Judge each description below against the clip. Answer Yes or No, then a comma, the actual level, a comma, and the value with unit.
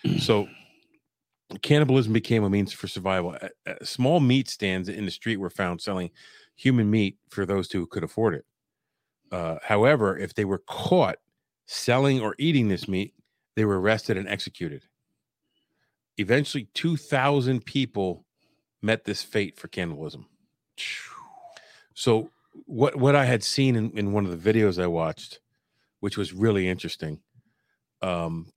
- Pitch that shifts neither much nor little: No, wide, 5.7 semitones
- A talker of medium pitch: No, low, 105 Hz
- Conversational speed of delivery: Yes, average, 145 wpm